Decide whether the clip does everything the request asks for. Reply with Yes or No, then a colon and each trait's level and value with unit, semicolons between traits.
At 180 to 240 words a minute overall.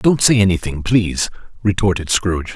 No: average, 140 wpm